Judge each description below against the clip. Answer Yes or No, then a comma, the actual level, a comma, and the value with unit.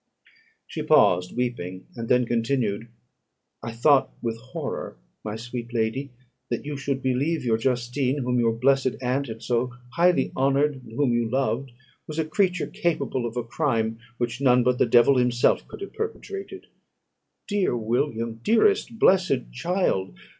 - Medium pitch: No, low, 125 Hz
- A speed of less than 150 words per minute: No, average, 155 wpm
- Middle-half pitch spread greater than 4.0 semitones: No, average, 3.5 semitones